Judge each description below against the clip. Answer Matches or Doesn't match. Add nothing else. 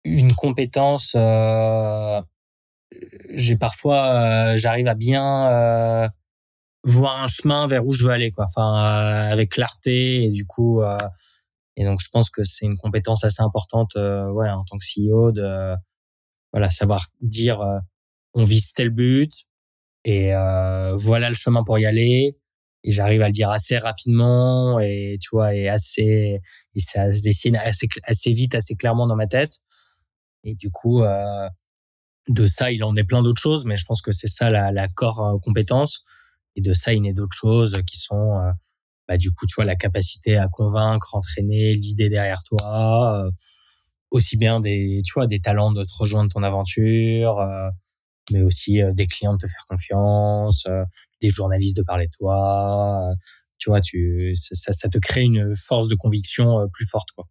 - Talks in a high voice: Doesn't match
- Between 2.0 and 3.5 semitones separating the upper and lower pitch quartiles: Matches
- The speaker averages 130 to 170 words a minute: Doesn't match